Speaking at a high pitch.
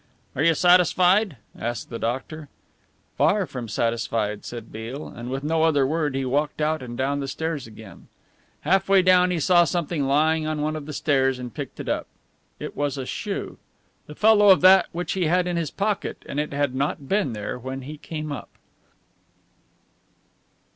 No: medium, 150 Hz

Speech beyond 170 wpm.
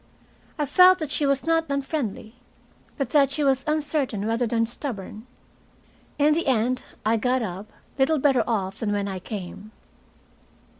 No: average, 155 wpm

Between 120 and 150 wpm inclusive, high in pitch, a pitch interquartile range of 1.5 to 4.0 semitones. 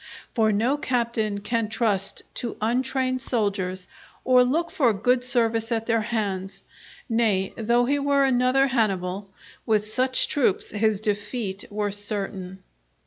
Yes: slow, 135 wpm; high, 225 Hz; average, 3.5 semitones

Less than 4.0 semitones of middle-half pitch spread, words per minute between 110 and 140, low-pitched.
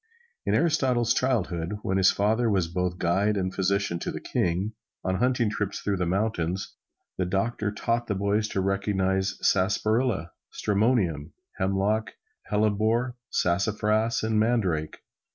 Yes: average, 2.9 semitones; slow, 135 wpm; low, 100 Hz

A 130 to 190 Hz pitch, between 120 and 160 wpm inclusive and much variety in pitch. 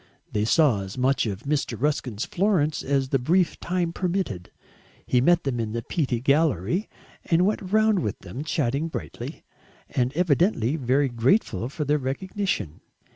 Yes: medium, 140 Hz; average, 155 wpm; wide, 6.3 semitones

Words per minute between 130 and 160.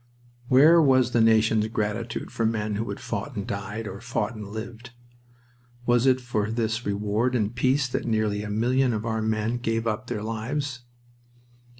No: average, 180 wpm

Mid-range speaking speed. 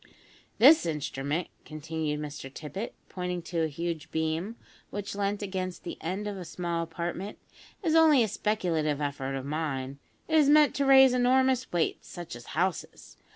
Yes: average, 160 wpm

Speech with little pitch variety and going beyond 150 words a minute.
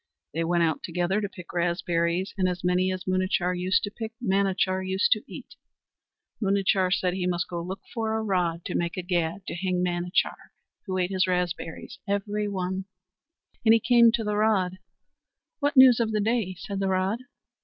Yes: narrow, 2.3 semitones; average, 185 wpm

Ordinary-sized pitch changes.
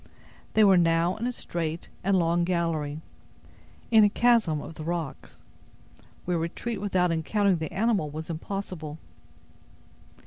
Yes: average, 3.7 semitones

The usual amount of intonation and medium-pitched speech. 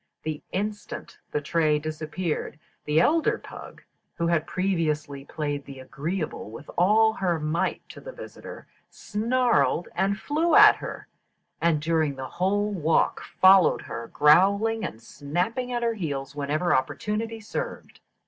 No: wide, 5.7 semitones; medium, 170 Hz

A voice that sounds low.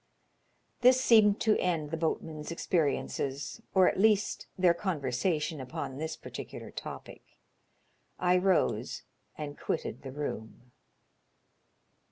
No: medium, 160 Hz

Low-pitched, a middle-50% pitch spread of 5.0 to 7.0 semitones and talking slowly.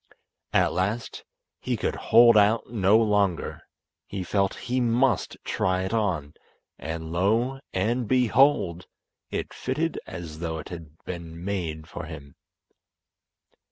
Yes: very low, 95 Hz; average, 5.3 semitones; slow, 125 wpm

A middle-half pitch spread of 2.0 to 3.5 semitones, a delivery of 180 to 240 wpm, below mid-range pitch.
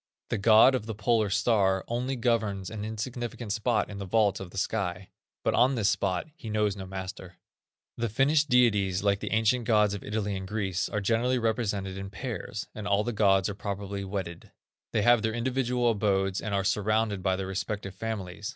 Yes: average, 2.8 semitones; average, 195 wpm; low, 105 Hz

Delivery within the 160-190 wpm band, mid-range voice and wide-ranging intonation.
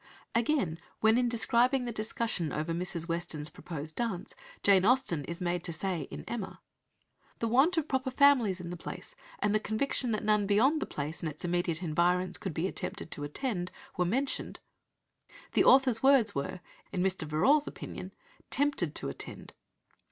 No: average, 170 wpm; high, 195 Hz; wide, 6.2 semitones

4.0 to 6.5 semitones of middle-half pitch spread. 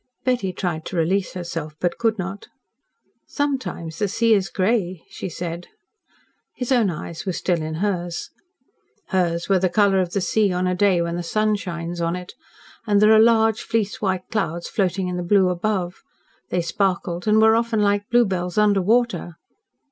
No: average, 3.4 semitones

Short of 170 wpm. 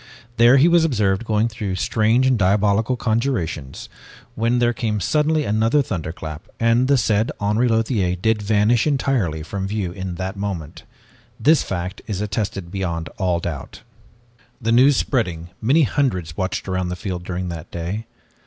Yes: average, 155 wpm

